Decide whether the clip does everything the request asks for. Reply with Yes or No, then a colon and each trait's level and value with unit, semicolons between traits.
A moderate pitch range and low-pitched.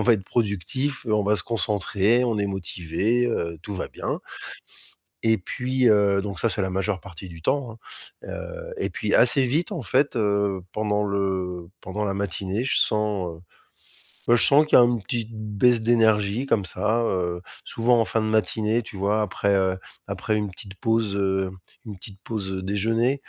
Yes: average, 3.2 semitones; low, 105 Hz